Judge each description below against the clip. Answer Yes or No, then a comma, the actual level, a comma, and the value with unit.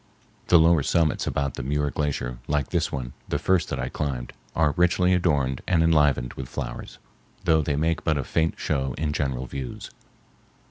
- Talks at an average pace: Yes, average, 180 wpm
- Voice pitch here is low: Yes, very low, 75 Hz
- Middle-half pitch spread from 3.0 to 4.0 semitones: Yes, average, 3.5 semitones